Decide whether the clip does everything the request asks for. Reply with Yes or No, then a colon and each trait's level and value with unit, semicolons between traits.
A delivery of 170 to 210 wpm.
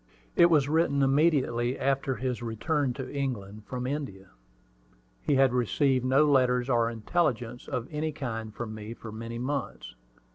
No: average, 150 wpm